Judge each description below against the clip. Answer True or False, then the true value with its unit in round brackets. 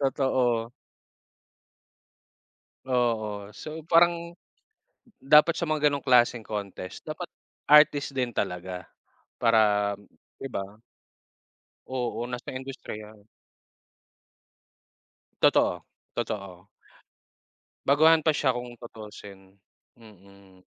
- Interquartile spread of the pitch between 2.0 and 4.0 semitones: False (5.6 semitones)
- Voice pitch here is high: False (120 Hz)